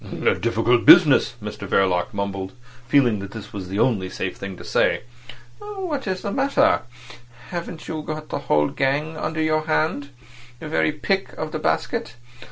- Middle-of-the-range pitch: Yes, medium, 145 Hz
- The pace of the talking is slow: No, average, 165 wpm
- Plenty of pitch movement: Yes, wide, 8.2 semitones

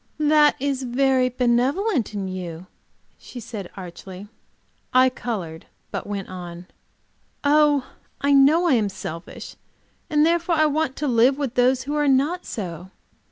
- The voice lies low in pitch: No, very high, 255 Hz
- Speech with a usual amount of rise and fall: No, wide, 6.7 semitones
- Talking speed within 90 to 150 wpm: Yes, average, 140 wpm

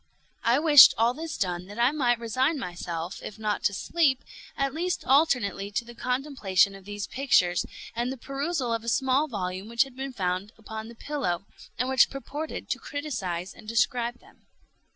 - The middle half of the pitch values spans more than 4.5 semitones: Yes, average, 5.2 semitones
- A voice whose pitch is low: No, high, 235 Hz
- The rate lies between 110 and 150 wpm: No, average, 180 wpm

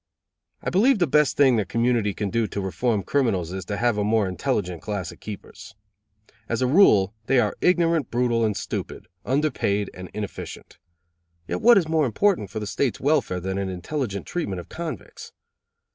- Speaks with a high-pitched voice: No, low, 115 Hz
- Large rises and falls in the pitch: Yes, wide, 6.4 semitones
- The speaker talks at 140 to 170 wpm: No, average, 185 wpm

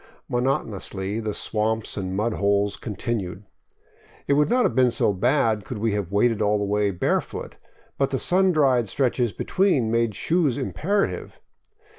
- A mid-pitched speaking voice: No, low, 115 Hz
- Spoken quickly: No, average, 155 wpm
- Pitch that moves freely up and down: No, average, 4.7 semitones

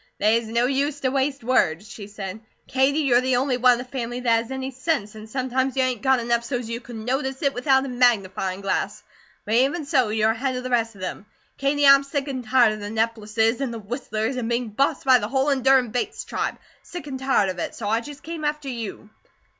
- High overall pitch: Yes, very high, 250 Hz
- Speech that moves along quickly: Yes, fast, 235 wpm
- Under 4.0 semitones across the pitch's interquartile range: Yes, average, 3.2 semitones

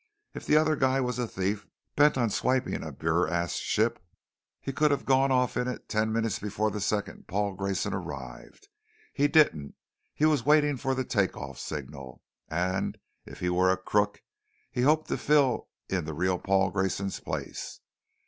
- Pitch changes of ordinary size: No, wide, 6.1 semitones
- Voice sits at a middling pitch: No, low, 110 Hz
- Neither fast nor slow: Yes, average, 175 wpm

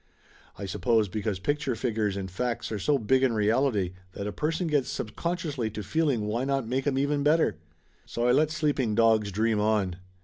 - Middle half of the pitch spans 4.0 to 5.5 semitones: Yes, average, 5.1 semitones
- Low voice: Yes, low, 115 Hz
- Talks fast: No, average, 195 wpm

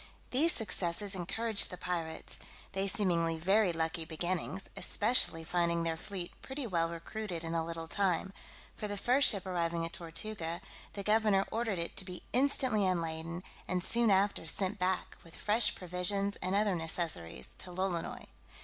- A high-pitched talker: No, medium, 180 Hz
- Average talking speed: Yes, average, 160 wpm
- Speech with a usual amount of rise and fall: Yes, average, 3.6 semitones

